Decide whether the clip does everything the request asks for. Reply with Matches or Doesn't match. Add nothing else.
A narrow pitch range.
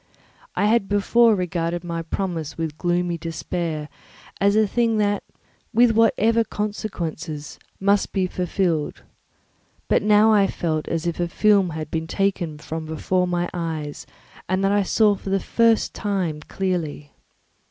Doesn't match